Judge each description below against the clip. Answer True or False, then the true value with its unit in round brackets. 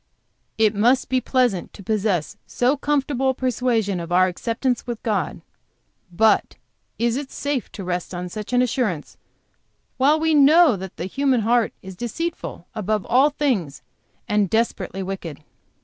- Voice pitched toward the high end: True (225 Hz)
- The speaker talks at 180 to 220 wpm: False (150 wpm)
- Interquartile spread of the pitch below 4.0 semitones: False (5.5 semitones)